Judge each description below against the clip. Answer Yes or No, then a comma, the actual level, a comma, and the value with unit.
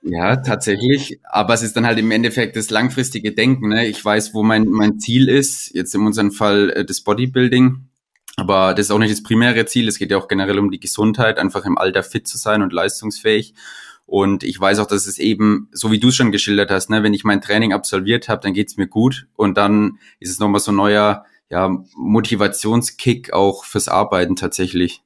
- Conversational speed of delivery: No, fast, 220 wpm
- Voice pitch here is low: Yes, low, 105 Hz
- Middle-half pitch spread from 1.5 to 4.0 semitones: Yes, narrow, 2.4 semitones